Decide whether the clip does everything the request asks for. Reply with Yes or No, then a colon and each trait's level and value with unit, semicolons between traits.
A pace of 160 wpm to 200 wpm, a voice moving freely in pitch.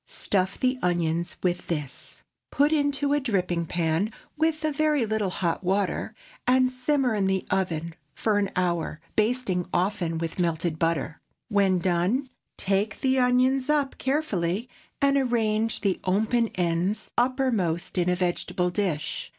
No: average, 140 wpm; wide, 6.5 semitones